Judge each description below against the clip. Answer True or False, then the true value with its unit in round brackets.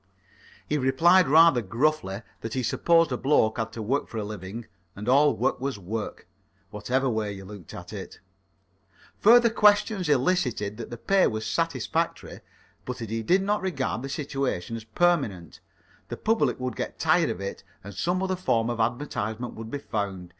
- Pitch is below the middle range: True (125 Hz)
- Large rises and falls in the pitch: True (6.0 semitones)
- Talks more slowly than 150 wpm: False (175 wpm)